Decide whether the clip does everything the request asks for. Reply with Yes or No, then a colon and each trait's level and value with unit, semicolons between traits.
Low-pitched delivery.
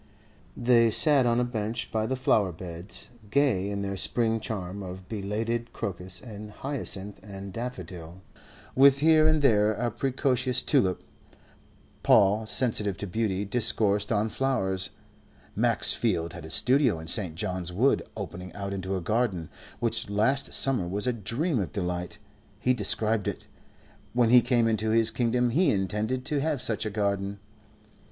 Yes: low, 110 Hz